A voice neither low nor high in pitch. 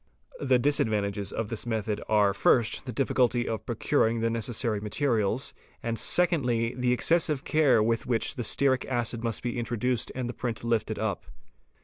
No: low, 115 Hz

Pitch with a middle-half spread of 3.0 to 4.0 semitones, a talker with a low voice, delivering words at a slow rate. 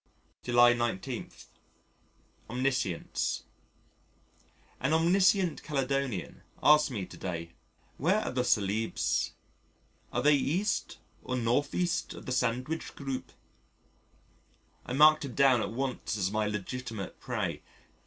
No: average, 4.5 semitones; low, 125 Hz; slow, 110 wpm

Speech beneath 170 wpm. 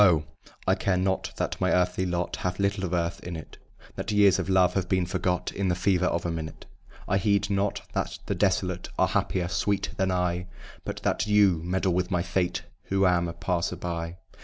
No: fast, 205 wpm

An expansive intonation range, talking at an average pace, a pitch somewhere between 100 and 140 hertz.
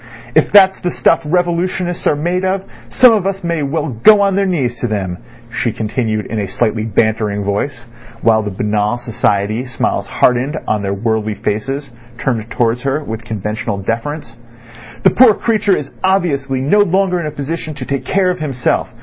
Yes: wide, 8.1 semitones; average, 180 wpm; low, 135 Hz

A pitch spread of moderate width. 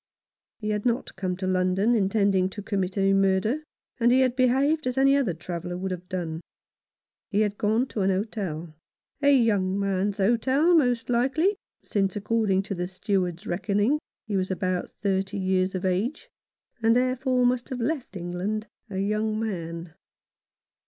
Yes: average, 4.4 semitones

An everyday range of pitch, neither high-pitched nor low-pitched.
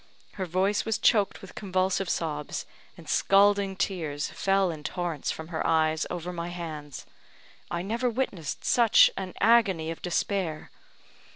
Yes: average, 3.6 semitones; medium, 180 Hz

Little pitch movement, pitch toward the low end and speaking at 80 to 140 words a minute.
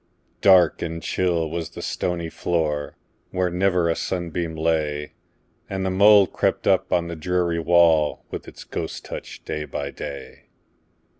Yes: narrow, 2.0 semitones; very low, 85 Hz; slow, 135 wpm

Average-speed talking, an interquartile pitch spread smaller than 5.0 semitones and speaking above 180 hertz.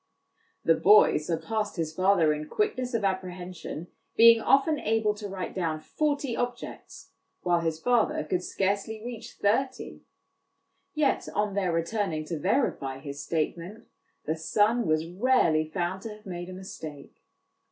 No: average, 145 wpm; wide, 5.5 semitones; high, 190 Hz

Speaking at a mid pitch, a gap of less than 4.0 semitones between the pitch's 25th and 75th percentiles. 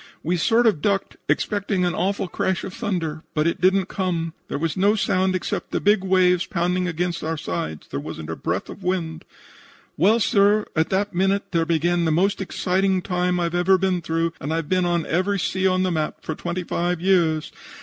Yes: medium, 180 Hz; narrow, 2.4 semitones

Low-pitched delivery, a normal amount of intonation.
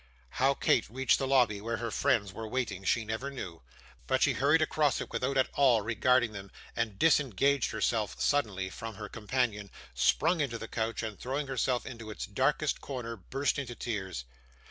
Yes: low, 120 Hz; average, 4.0 semitones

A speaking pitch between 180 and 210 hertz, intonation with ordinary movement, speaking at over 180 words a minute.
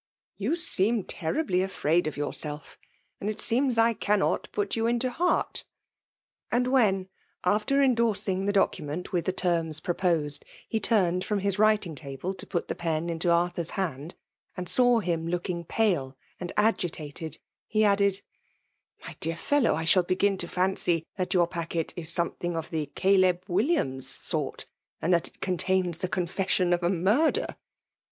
No: medium, 185 Hz; average, 3.8 semitones; average, 160 wpm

